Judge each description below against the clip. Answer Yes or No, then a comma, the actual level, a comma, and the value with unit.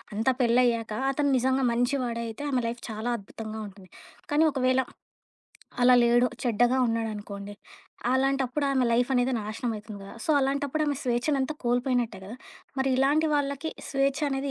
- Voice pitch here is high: Yes, very high, 250 Hz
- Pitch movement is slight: No, average, 3.0 semitones